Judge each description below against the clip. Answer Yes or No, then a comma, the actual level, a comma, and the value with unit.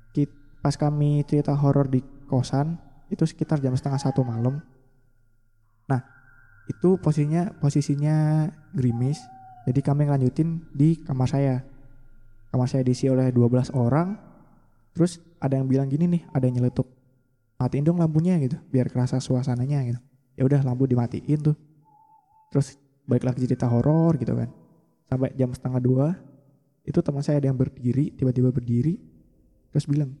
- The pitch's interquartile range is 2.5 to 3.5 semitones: Yes, average, 2.8 semitones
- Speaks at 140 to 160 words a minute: Yes, average, 145 wpm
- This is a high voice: No, low, 135 Hz